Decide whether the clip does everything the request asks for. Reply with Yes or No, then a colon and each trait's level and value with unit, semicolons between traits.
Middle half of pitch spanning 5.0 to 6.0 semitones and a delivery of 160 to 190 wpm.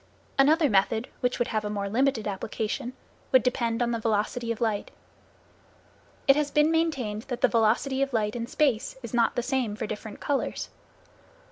No: average, 3.8 semitones; average, 175 wpm